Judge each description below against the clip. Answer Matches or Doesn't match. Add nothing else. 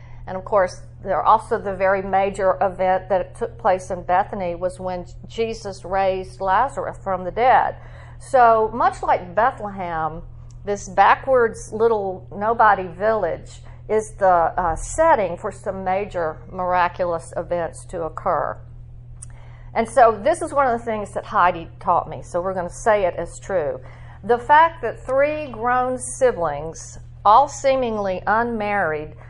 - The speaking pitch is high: Matches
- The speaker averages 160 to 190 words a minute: Doesn't match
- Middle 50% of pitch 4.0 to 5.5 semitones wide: Matches